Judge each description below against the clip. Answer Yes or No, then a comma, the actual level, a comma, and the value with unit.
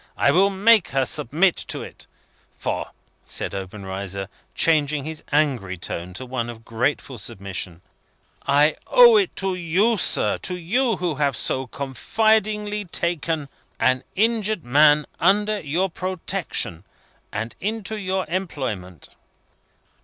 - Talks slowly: Yes, slow, 130 wpm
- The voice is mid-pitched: Yes, medium, 155 Hz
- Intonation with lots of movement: Yes, wide, 8.1 semitones